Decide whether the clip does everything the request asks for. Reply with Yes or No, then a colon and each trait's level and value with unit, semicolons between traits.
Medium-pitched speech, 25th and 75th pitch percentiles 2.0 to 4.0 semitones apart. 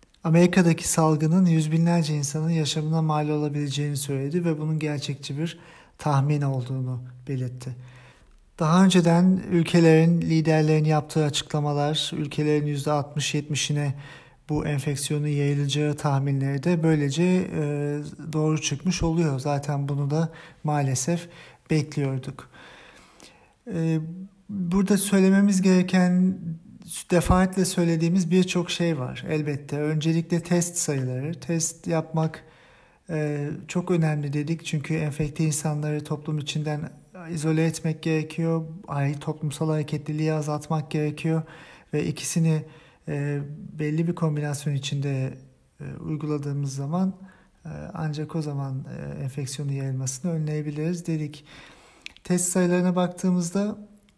Yes: medium, 155 Hz; narrow, 2.5 semitones